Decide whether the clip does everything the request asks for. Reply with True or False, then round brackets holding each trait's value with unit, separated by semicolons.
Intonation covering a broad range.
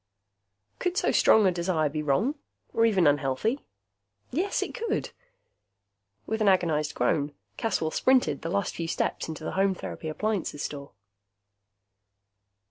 True (6.4 semitones)